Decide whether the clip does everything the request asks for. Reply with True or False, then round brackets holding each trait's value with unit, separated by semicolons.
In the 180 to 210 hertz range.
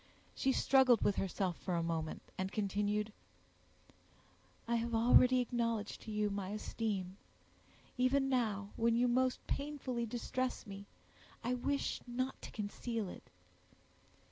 False (230 Hz)